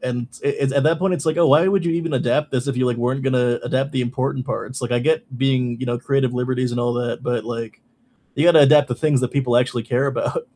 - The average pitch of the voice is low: Yes, low, 130 Hz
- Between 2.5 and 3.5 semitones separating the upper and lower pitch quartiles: Yes, average, 2.9 semitones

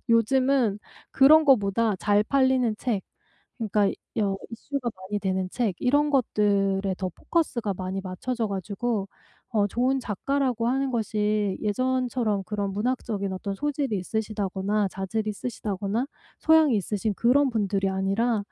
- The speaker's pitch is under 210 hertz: No, high, 215 Hz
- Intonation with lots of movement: No, average, 4.2 semitones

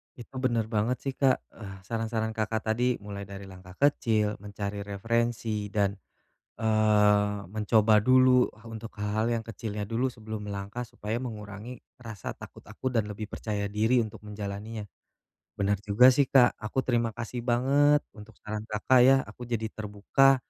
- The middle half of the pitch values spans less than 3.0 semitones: Yes, narrow, 2.5 semitones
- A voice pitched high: No, low, 110 Hz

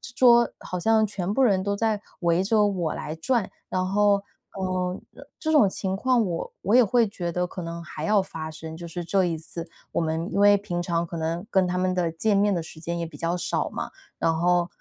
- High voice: No, medium, 180 Hz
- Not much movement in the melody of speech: No, average, 3.3 semitones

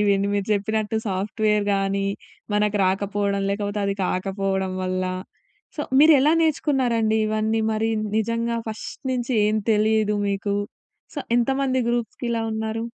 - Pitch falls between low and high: No, high, 215 Hz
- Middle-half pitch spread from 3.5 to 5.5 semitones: No, narrow, 2.5 semitones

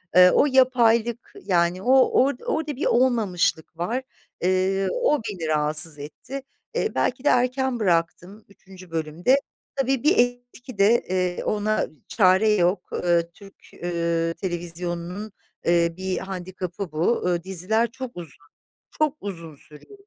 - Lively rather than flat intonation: Yes, wide, 5.8 semitones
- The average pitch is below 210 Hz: Yes, high, 190 Hz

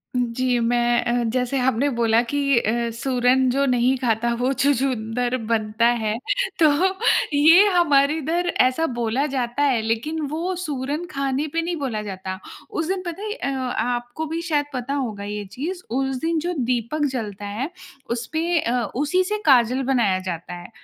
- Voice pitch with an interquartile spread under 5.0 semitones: Yes, average, 4.2 semitones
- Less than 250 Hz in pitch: No, very high, 255 Hz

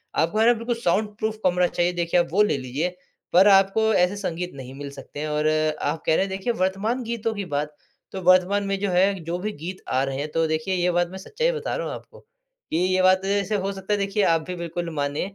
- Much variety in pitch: No, average, 3.9 semitones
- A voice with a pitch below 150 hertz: No, medium, 185 Hz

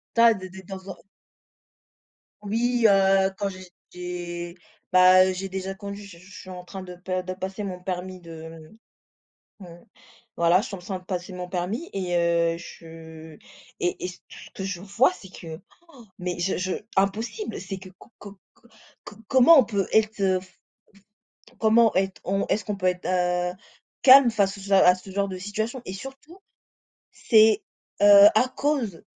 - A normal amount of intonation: No, narrow, 2.3 semitones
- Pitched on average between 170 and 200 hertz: Yes, high, 190 Hz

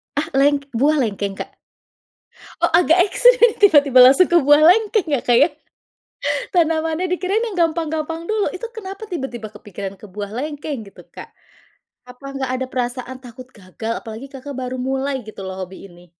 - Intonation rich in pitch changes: Yes, wide, 5.9 semitones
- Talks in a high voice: Yes, very high, 275 Hz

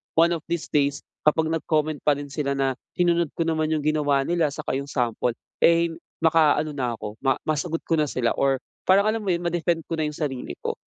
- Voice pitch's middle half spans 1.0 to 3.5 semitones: Yes, average, 3.1 semitones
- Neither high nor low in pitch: Yes, medium, 155 Hz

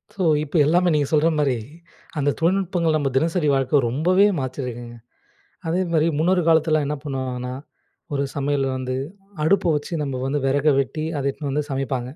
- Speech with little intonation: No, average, 3.3 semitones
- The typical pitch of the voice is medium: Yes, medium, 145 Hz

